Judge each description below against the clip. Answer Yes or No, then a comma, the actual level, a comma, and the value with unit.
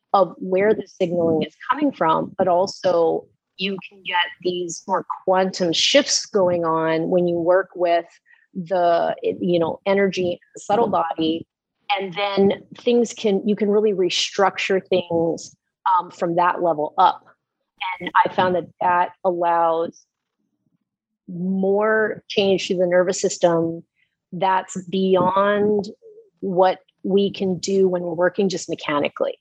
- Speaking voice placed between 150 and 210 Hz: Yes, medium, 185 Hz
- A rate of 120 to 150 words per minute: Yes, slow, 135 wpm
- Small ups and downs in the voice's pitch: Yes, narrow, 2.1 semitones